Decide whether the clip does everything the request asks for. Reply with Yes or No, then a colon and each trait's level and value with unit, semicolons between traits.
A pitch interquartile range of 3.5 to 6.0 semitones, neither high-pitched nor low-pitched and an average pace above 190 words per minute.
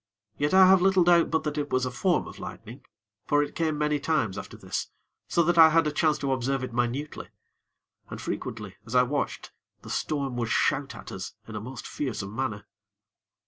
Yes: average, 4.5 semitones; medium, 145 Hz; average, 200 wpm